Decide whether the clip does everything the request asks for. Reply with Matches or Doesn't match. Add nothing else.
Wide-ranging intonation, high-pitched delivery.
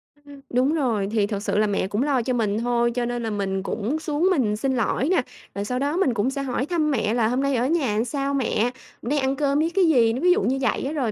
Doesn't match